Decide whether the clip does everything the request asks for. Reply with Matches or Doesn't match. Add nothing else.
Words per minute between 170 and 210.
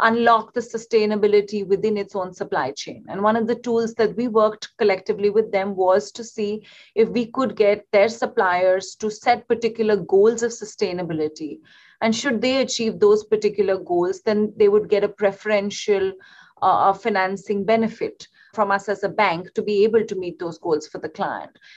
Matches